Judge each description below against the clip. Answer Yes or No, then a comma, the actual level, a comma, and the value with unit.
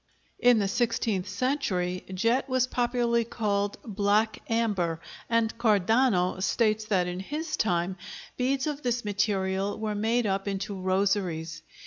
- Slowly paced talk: Yes, slow, 130 wpm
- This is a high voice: Yes, high, 210 Hz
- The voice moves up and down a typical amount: Yes, average, 3.8 semitones